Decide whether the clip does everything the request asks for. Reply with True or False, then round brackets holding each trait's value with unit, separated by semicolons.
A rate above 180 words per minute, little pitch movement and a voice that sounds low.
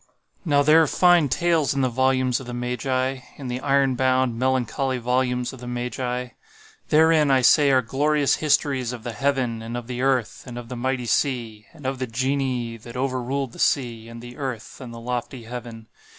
True (195 wpm; 2.0 semitones; 130 Hz)